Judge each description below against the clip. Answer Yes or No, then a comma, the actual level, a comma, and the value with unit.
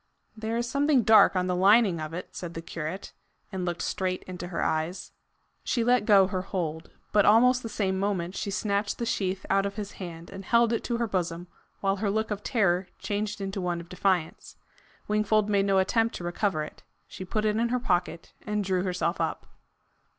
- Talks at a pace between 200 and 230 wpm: Yes, fast, 205 wpm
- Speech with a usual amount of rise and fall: Yes, average, 3.0 semitones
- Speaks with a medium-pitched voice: No, high, 195 Hz